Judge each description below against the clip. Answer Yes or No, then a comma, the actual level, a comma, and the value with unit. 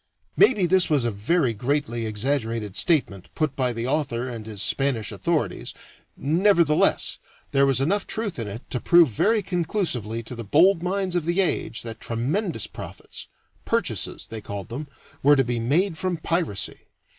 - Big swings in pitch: Yes, wide, 7.0 semitones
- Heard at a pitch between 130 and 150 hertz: Yes, medium, 140 Hz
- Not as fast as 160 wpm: No, average, 165 wpm